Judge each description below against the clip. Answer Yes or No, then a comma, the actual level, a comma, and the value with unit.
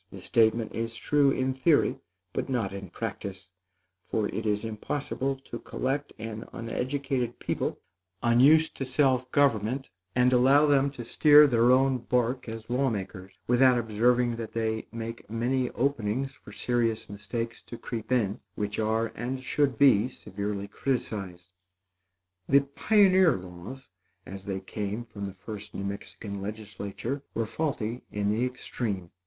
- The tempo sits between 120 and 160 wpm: Yes, average, 145 wpm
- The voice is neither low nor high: No, low, 115 Hz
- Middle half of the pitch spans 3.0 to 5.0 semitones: Yes, average, 3.9 semitones